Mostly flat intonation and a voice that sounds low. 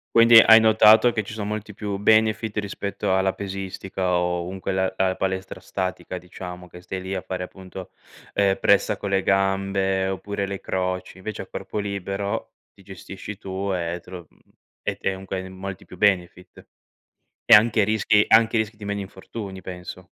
Yes: narrow, 1.7 semitones; very low, 95 Hz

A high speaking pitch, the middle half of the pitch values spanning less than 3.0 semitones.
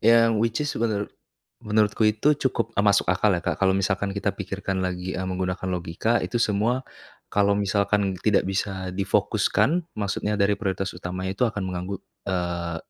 No: low, 100 Hz; narrow, 2.4 semitones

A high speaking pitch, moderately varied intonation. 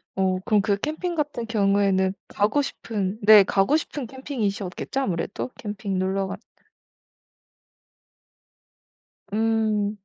Yes: high, 210 Hz; average, 3.1 semitones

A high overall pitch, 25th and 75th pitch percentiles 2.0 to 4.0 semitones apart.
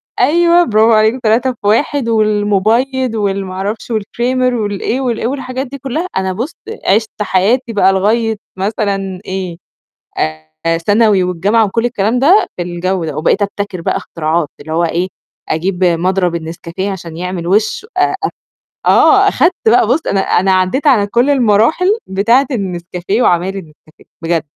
No: high, 205 Hz; average, 4.5 semitones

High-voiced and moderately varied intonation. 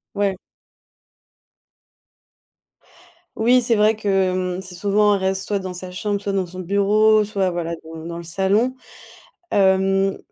No: high, 195 Hz; narrow, 2.1 semitones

